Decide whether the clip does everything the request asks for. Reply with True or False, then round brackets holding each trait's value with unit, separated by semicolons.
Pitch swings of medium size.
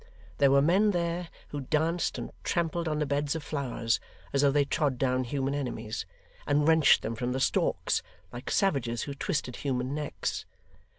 True (3.6 semitones)